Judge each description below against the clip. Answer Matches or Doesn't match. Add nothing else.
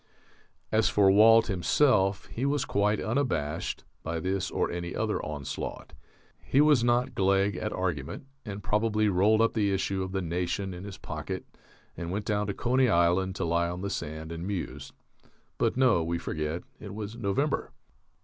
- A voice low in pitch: Matches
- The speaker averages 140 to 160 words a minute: Doesn't match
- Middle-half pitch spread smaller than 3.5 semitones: Doesn't match